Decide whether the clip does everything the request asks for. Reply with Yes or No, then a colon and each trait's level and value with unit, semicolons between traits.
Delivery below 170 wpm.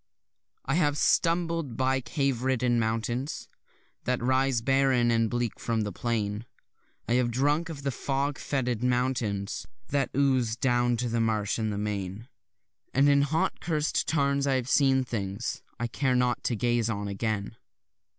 Yes: average, 160 wpm